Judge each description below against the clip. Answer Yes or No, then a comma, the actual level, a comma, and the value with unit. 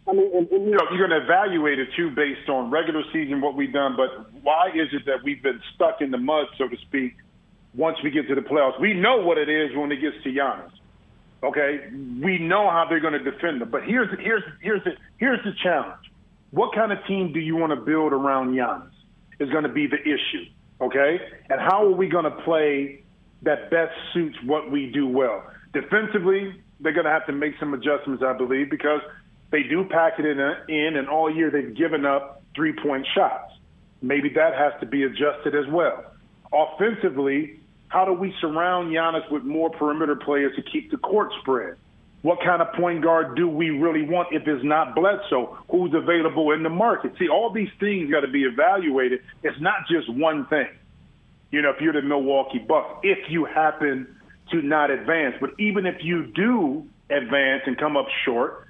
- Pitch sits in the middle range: Yes, medium, 155 Hz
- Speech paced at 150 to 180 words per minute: No, fast, 205 wpm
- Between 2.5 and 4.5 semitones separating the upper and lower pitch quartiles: Yes, average, 4.0 semitones